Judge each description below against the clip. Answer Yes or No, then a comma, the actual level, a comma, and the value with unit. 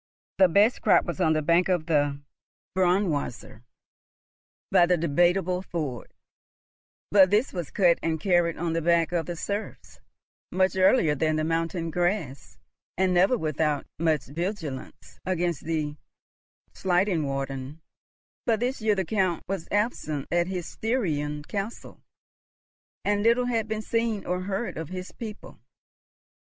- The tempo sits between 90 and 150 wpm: Yes, average, 140 wpm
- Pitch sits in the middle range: Yes, medium, 175 Hz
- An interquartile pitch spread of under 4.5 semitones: Yes, average, 3.9 semitones